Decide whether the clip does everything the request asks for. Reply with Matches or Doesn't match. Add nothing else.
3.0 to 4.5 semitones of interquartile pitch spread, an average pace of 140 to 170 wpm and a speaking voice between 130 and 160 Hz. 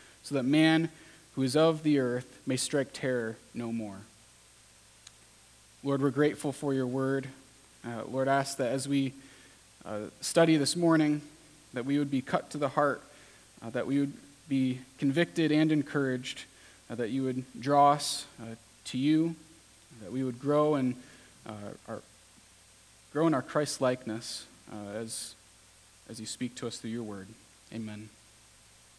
Matches